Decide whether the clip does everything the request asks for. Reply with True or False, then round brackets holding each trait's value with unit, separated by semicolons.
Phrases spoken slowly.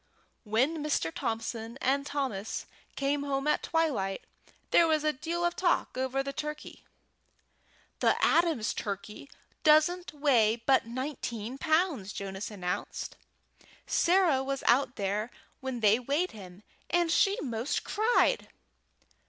True (125 wpm)